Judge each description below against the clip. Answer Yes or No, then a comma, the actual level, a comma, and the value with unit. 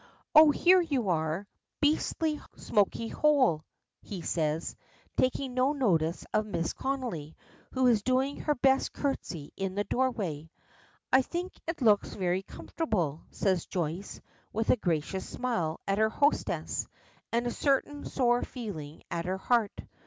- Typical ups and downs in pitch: No, wide, 7.3 semitones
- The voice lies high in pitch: Yes, high, 220 Hz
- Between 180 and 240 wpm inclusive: No, average, 140 wpm